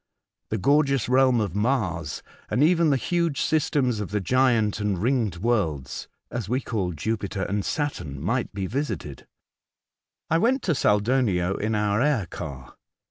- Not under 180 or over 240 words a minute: No, average, 155 wpm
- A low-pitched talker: Yes, low, 110 Hz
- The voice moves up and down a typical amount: No, wide, 5.8 semitones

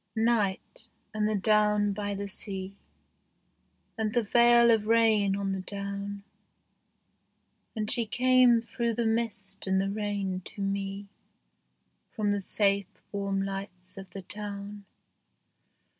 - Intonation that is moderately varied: No, narrow, 1.9 semitones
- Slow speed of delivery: Yes, slow, 130 wpm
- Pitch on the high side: Yes, high, 205 Hz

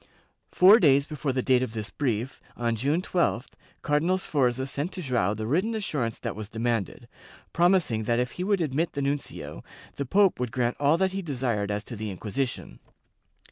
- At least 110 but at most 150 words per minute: No, average, 185 wpm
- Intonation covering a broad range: Yes, wide, 6.1 semitones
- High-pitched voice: No, low, 135 Hz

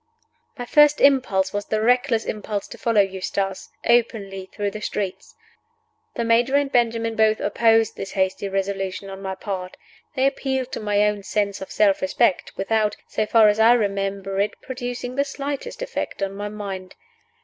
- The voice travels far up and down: No, average, 3.4 semitones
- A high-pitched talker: Yes, high, 210 Hz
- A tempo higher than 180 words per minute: No, average, 170 wpm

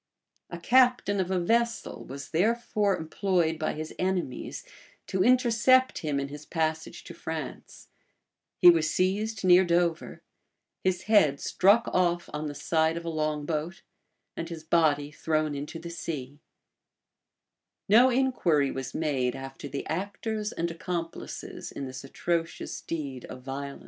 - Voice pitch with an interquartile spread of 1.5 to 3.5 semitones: No, average, 4.2 semitones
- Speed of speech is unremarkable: Yes, average, 145 wpm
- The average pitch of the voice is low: No, medium, 165 Hz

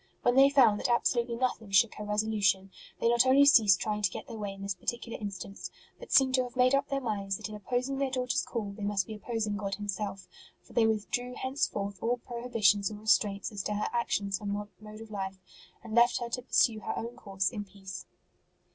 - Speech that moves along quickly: Yes, fast, 225 wpm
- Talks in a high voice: Yes, high, 215 Hz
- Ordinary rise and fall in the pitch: Yes, average, 3.2 semitones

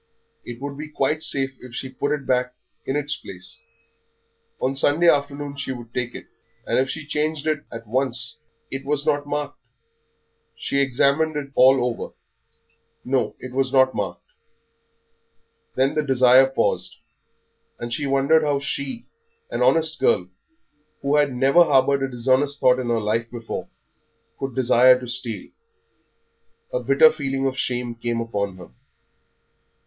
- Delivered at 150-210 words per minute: Yes, average, 155 wpm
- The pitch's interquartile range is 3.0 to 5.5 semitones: No, narrow, 2.6 semitones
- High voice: No, low, 135 Hz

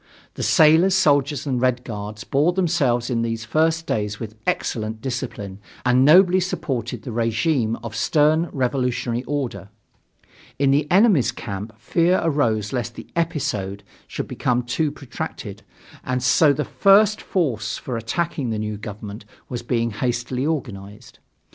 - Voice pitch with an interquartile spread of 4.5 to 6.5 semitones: Yes, average, 5.2 semitones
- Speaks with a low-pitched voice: Yes, low, 125 Hz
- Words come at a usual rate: Yes, average, 145 wpm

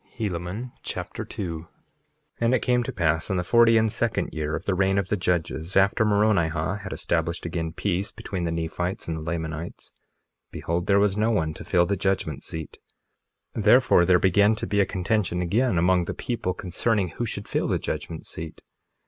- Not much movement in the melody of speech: No, average, 3.7 semitones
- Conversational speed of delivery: Yes, average, 190 wpm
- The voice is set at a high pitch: No, very low, 95 Hz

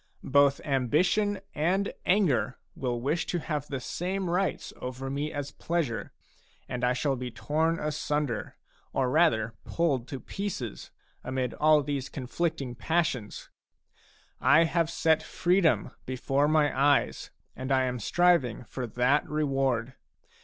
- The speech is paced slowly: Yes, slow, 130 wpm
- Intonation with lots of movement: No, average, 4.3 semitones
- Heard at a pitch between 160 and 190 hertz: No, medium, 145 Hz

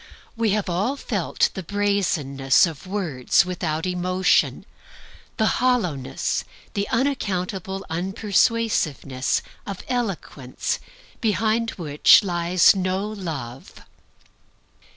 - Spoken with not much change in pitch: No, average, 4.3 semitones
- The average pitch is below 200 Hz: Yes, medium, 185 Hz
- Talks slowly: Yes, slow, 90 wpm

